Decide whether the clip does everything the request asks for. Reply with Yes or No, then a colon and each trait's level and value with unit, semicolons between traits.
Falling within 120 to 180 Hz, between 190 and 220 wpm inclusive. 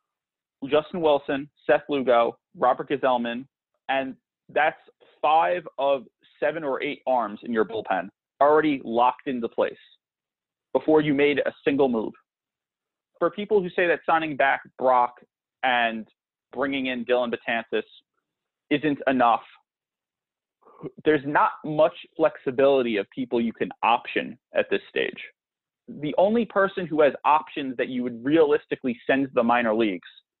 No: medium, 140 Hz; slow, 135 wpm